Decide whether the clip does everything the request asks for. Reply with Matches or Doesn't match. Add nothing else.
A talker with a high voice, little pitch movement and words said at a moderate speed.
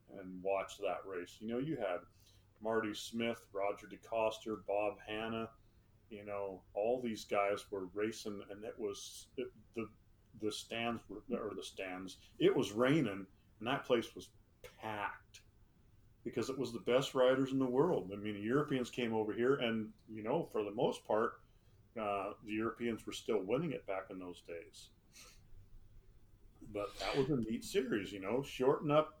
Doesn't match